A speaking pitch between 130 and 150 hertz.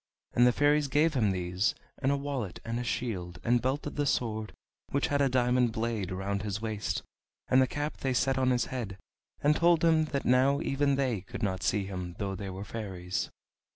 No: low, 120 Hz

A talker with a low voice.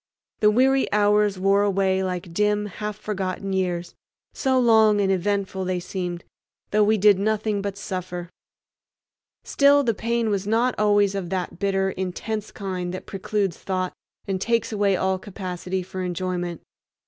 No: high, 195 Hz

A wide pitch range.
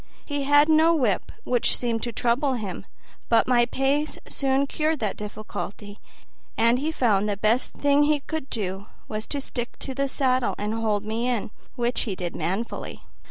No: average, 4.6 semitones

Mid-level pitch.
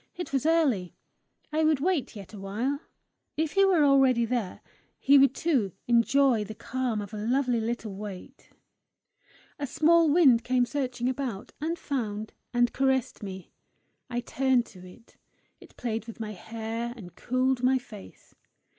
No: high, 245 Hz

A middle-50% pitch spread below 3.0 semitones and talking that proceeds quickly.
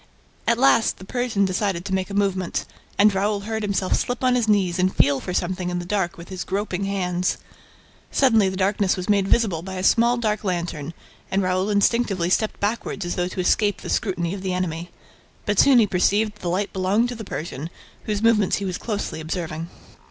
Yes: narrow, 2.6 semitones; fast, 210 wpm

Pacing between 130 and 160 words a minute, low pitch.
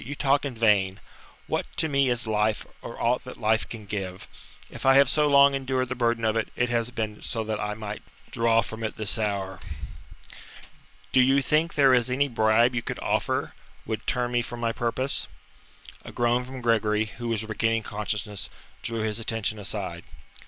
No: average, 190 wpm; low, 115 Hz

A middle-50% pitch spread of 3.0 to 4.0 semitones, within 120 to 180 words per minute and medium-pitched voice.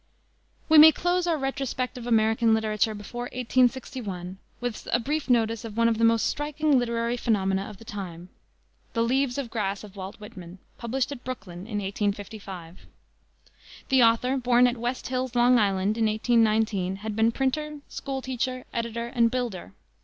No: average, 3.3 semitones; average, 165 wpm; high, 230 Hz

